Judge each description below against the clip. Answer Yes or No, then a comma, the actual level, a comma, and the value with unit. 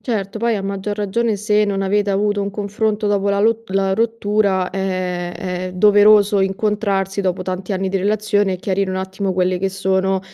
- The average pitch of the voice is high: Yes, high, 195 Hz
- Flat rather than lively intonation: Yes, narrow, 1.6 semitones